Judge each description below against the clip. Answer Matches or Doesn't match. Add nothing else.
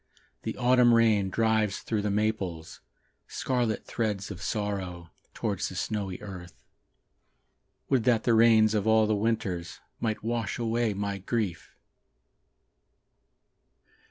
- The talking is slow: Matches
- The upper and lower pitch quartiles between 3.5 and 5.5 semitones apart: Doesn't match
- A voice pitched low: Matches